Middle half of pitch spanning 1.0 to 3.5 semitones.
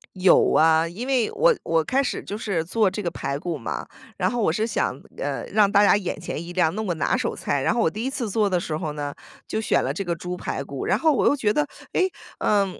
No: average, 5.3 semitones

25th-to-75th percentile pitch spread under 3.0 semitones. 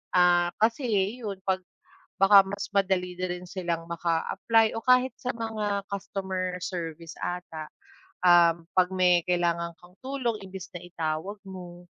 Yes: narrow, 2.5 semitones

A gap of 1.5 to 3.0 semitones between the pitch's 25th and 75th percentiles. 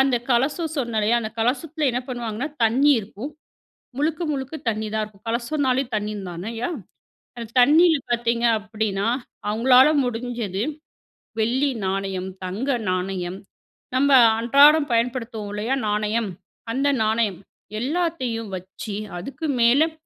No: average, 4.2 semitones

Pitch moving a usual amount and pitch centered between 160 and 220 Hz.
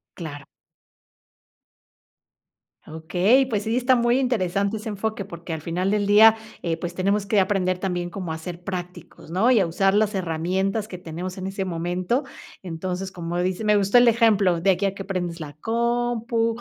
Yes: average, 3.7 semitones; high, 190 Hz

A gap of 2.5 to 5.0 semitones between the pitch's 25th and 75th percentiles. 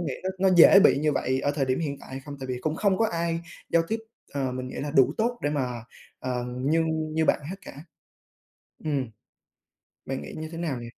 Yes: average, 4.2 semitones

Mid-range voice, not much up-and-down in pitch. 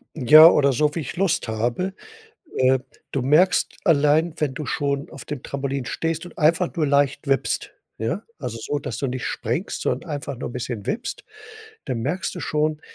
No: medium, 145 Hz; average, 3.5 semitones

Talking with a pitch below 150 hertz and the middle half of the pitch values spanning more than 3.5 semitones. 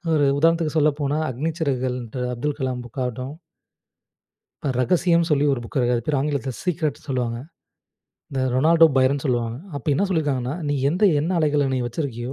No: medium, 140 Hz; average, 3.2 semitones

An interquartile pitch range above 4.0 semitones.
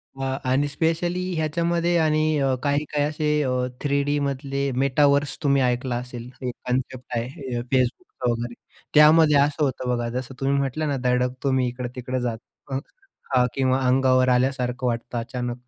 No: narrow, 2.6 semitones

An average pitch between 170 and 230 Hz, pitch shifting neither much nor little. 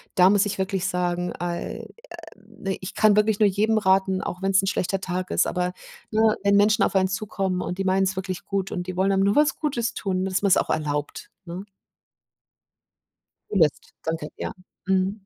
No: high, 190 Hz; narrow, 1.8 semitones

